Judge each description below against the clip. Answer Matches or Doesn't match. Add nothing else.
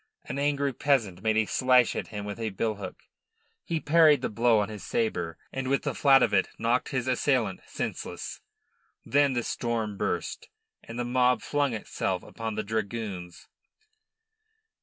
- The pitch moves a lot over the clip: Doesn't match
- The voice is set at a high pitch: Doesn't match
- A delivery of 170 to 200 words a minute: Doesn't match